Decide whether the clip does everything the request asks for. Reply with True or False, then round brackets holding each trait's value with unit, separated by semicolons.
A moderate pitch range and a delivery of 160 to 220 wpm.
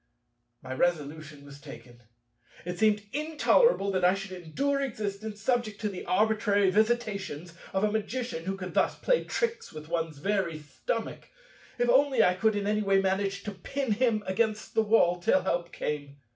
True (4.0 semitones; 170 wpm)